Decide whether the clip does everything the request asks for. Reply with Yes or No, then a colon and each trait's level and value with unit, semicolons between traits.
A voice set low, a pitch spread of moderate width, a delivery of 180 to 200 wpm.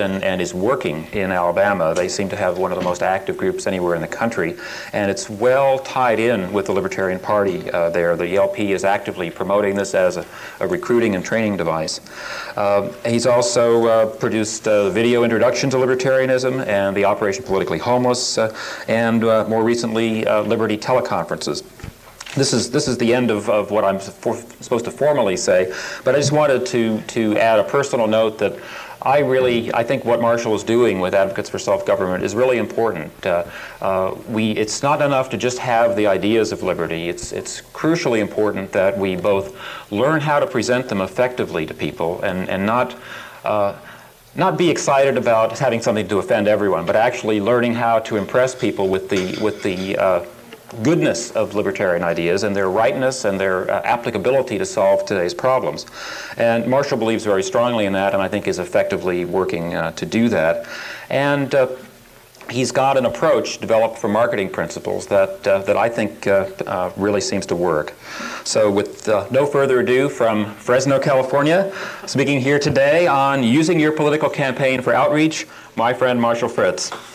Yes: low, 115 Hz; average, 4.2 semitones; average, 185 wpm